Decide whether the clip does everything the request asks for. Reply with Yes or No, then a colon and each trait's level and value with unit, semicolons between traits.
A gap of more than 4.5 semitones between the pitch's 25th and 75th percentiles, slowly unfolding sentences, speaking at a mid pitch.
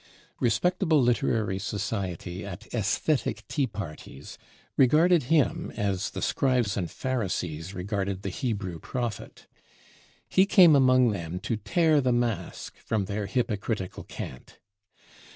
No: average, 5.1 semitones; slow, 115 wpm; low, 110 Hz